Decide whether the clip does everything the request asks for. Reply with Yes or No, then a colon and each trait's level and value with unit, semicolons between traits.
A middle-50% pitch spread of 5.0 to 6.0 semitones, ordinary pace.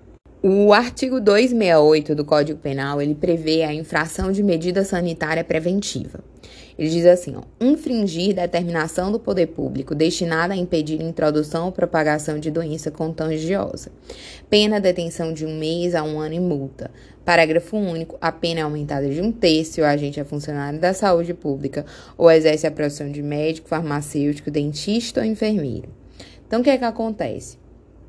No: average, 3.2 semitones; average, 165 wpm